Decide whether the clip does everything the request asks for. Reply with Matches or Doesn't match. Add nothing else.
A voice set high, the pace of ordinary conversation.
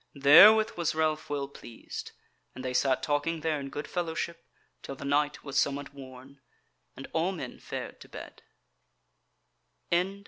Doesn't match